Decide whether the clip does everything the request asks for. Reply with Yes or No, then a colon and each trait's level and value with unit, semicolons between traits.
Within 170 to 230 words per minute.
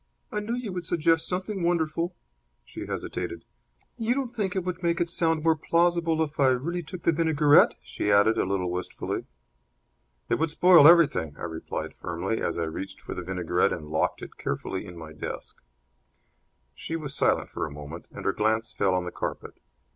Yes: average, 190 wpm